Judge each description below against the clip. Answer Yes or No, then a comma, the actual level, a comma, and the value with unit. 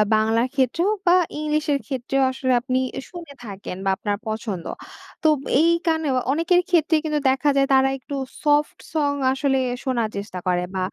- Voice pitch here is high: Yes, very high, 270 Hz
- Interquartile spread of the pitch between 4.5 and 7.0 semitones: Yes, average, 4.9 semitones